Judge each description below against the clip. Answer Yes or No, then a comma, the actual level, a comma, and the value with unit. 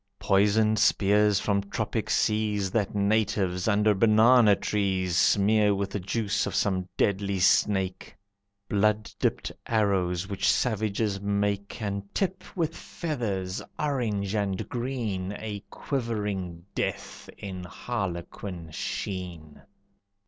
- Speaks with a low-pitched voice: Yes, low, 100 Hz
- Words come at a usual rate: No, slow, 110 wpm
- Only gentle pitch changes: Yes, narrow, 2.1 semitones